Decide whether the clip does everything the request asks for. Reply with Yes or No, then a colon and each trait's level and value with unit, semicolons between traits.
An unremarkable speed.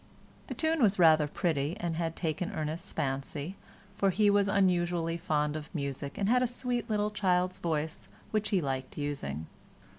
Yes: average, 170 wpm